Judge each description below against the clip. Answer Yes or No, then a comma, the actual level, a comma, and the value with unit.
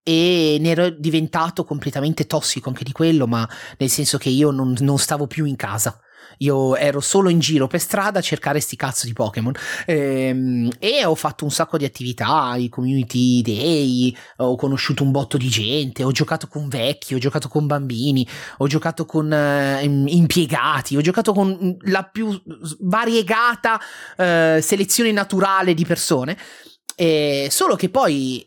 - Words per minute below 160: No, average, 165 wpm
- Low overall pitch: No, medium, 150 Hz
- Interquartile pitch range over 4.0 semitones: No, average, 3.7 semitones